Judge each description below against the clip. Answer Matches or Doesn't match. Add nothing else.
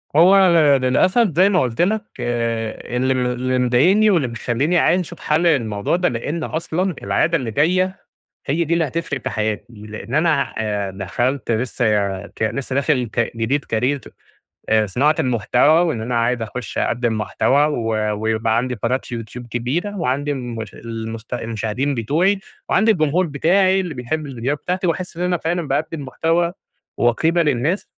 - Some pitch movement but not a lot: Doesn't match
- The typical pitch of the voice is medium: Doesn't match